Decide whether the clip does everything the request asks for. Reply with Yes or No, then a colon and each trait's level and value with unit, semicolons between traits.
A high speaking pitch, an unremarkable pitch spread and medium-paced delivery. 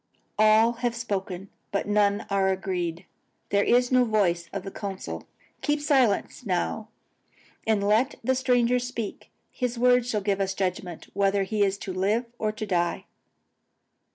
Yes: high, 205 Hz; average, 3.7 semitones; average, 155 wpm